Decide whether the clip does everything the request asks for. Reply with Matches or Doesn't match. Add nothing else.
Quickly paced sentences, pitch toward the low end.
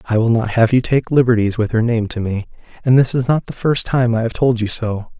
Matches